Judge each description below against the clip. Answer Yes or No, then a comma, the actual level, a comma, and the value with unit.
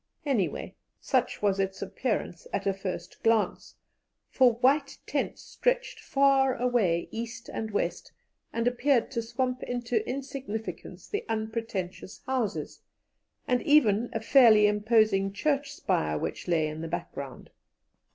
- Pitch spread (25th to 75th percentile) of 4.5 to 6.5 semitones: Yes, average, 4.8 semitones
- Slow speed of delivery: Yes, slow, 130 wpm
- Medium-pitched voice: No, high, 225 Hz